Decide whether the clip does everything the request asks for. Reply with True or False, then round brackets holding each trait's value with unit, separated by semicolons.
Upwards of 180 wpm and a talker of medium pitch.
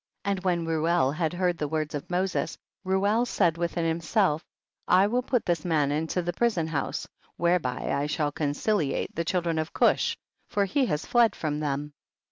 False (175 wpm; 170 Hz)